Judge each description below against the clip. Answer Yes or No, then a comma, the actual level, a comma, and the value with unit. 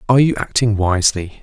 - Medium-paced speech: Yes, average, 170 wpm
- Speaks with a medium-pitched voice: No, low, 110 Hz